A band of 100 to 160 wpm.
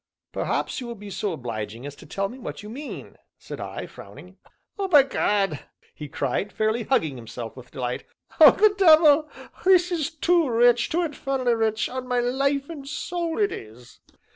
No: average, 180 wpm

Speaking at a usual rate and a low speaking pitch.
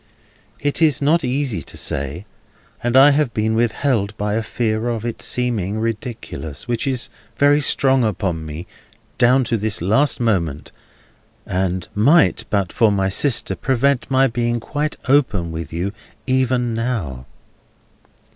Yes: average, 145 wpm; low, 115 Hz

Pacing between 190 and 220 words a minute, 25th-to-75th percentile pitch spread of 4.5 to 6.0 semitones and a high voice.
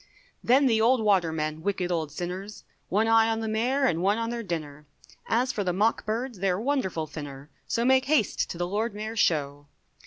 Yes: average, 195 wpm; wide, 5.4 semitones; high, 205 Hz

